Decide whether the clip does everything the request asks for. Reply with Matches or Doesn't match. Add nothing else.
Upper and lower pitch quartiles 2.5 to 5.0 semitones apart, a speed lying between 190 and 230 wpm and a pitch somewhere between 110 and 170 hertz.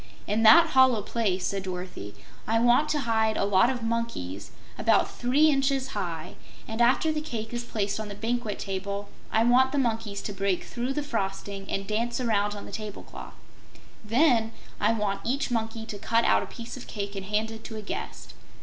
Doesn't match